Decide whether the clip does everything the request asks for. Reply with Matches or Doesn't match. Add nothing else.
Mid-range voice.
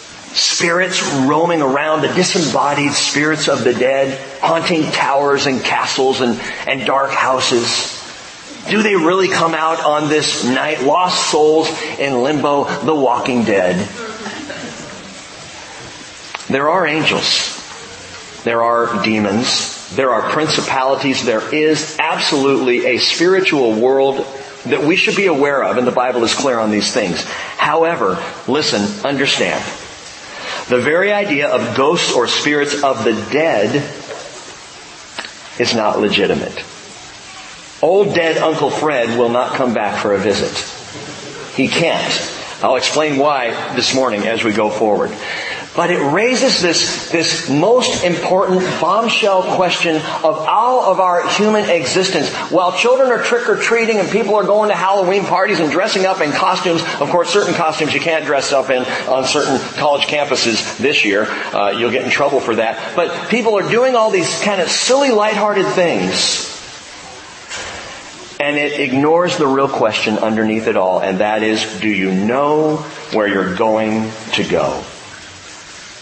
Matches